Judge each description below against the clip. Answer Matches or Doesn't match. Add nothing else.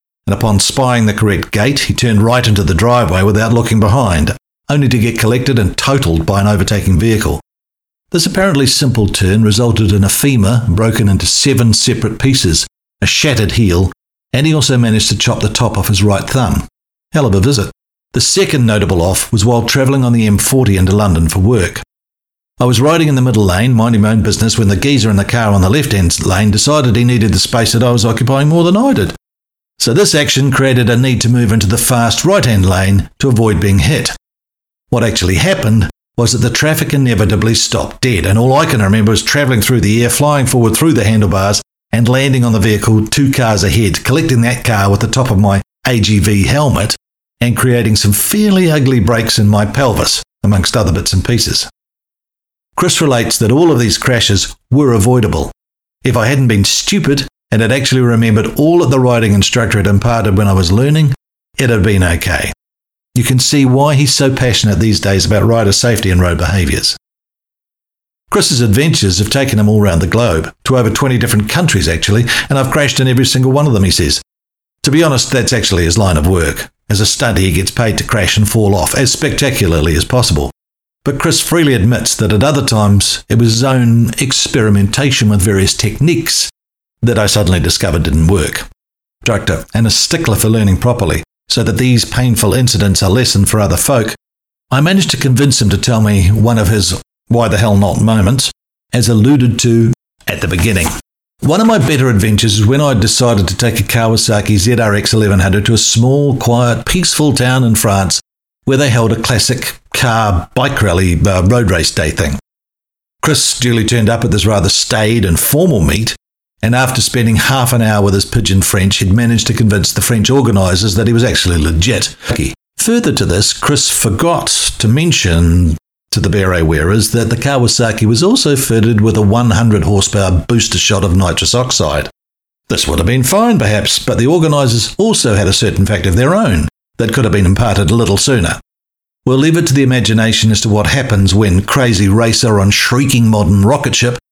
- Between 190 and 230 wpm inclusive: Matches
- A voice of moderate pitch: Doesn't match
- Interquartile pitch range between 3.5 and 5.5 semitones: Matches